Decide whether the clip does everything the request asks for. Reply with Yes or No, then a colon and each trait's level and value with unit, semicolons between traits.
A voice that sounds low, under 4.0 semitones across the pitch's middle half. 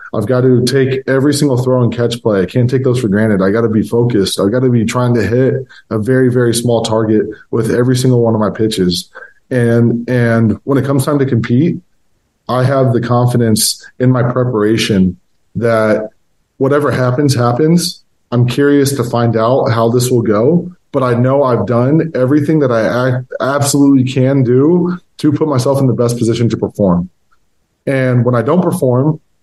Yes: low, 125 Hz; average, 2.8 semitones